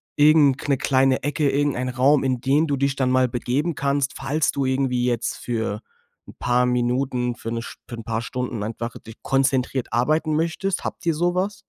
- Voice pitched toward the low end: Yes, low, 130 Hz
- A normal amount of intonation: Yes, average, 3.0 semitones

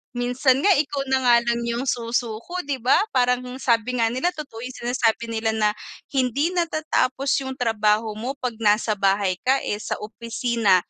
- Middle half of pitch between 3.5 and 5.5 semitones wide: No, average, 2.9 semitones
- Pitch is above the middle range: Yes, high, 245 Hz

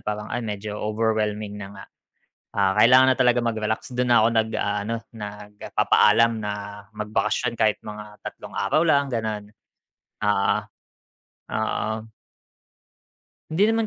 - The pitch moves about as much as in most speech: No, narrow, 2.1 semitones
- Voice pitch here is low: Yes, low, 110 Hz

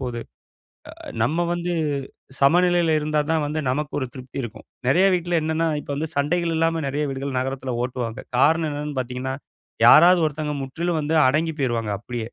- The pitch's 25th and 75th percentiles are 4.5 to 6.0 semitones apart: No, average, 3.9 semitones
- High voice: No, medium, 150 Hz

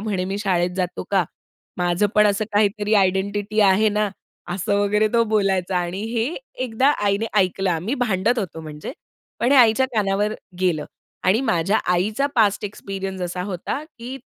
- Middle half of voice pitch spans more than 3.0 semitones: No, average, 2.7 semitones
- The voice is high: Yes, high, 200 Hz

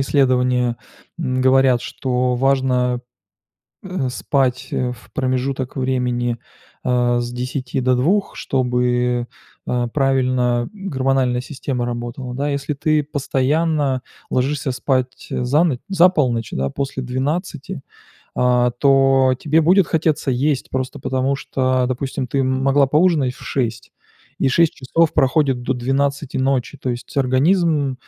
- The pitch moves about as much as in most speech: No, narrow, 2.1 semitones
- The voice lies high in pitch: No, low, 130 Hz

